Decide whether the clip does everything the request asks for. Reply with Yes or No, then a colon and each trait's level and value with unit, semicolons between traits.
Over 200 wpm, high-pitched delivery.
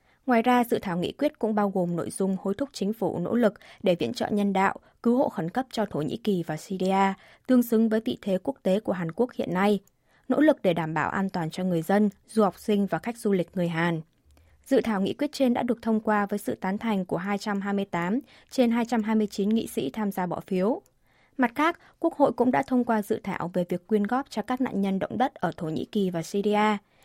Yes: fast, 250 wpm; high, 205 Hz